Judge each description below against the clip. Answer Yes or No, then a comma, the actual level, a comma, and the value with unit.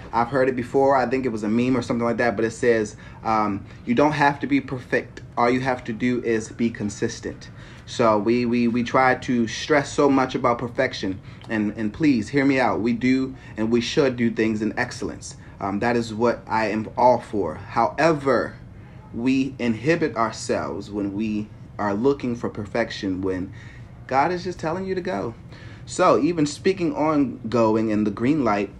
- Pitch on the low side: Yes, low, 120 Hz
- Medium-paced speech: Yes, average, 195 wpm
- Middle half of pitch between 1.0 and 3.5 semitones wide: Yes, average, 3.0 semitones